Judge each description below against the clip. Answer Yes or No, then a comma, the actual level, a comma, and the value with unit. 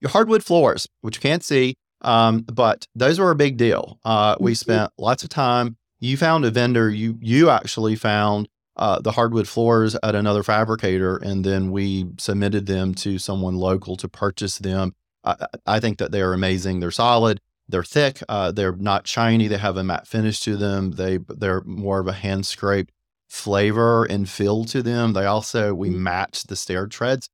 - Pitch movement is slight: No, average, 3.3 semitones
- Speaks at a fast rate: No, average, 190 wpm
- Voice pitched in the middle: No, low, 105 Hz